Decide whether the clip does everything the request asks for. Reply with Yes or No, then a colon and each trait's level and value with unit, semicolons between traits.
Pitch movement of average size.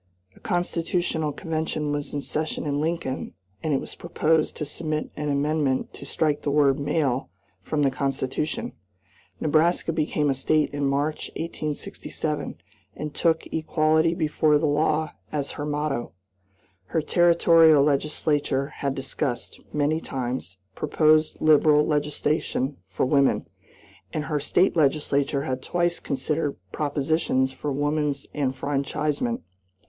No: narrow, 2.0 semitones